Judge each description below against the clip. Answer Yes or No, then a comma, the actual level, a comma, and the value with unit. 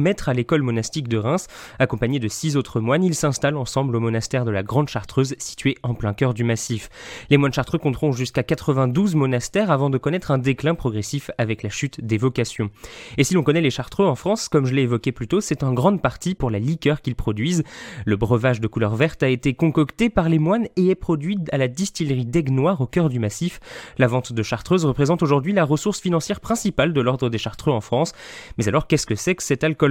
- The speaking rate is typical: No, fast, 225 wpm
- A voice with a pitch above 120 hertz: Yes, medium, 140 Hz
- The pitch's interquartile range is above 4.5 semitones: Yes, average, 5.0 semitones